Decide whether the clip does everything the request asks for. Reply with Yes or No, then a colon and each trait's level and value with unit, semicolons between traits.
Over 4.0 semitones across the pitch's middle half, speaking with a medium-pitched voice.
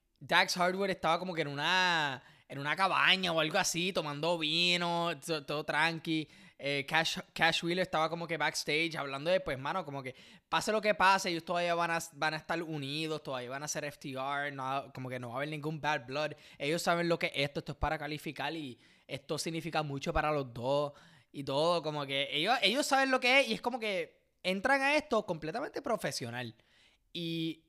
No: average, 3.3 semitones; medium, 160 Hz